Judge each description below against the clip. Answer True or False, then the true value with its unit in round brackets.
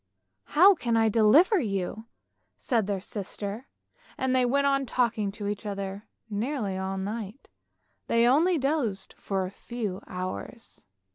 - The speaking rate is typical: True (155 wpm)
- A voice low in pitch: False (220 Hz)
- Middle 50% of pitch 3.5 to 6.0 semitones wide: True (4.7 semitones)